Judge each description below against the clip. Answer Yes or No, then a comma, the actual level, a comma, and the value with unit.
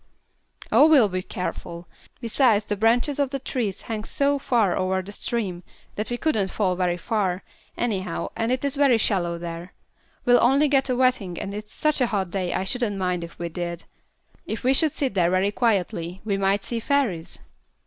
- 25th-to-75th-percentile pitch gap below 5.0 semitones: No, wide, 5.4 semitones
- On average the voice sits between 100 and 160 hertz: No, high, 205 Hz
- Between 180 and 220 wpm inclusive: Yes, average, 190 wpm